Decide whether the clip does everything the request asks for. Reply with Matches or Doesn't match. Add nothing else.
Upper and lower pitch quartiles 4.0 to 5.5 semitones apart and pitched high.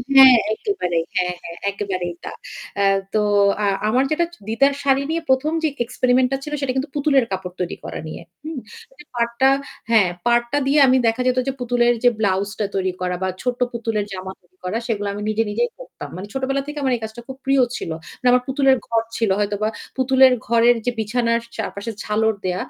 Matches